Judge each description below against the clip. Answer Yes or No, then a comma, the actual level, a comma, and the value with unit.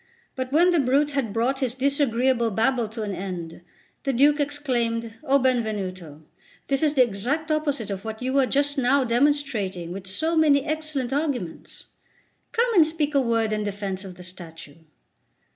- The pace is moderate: Yes, average, 170 wpm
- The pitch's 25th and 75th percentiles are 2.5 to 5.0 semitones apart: No, wide, 5.6 semitones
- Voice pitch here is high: Yes, very high, 255 Hz